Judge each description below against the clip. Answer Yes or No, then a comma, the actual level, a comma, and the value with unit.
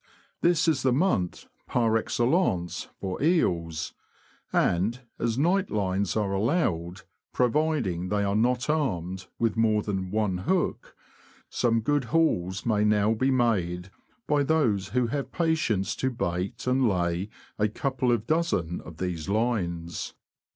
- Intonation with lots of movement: Yes, wide, 6.0 semitones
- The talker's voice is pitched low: Yes, low, 110 Hz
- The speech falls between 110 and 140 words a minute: Yes, slow, 135 wpm